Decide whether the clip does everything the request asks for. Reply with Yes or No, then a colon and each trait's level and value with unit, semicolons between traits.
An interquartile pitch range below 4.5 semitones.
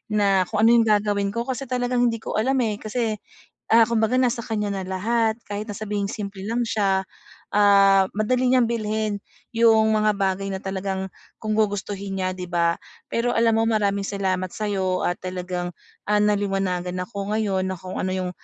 Yes: narrow, 2.6 semitones